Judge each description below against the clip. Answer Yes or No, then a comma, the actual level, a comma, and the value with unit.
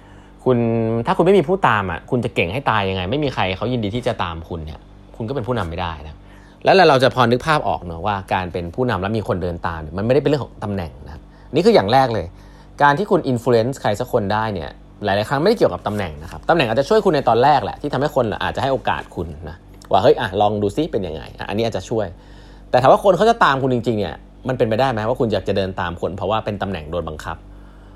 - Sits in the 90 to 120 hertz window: Yes, low, 105 Hz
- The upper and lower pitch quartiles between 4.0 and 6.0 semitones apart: Yes, average, 5.2 semitones